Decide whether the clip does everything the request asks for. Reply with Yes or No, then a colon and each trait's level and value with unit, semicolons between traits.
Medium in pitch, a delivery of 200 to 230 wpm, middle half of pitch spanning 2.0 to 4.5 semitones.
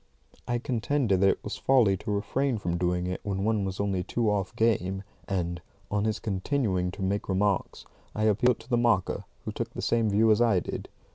No: low, 100 Hz; fast, 205 wpm; average, 3.3 semitones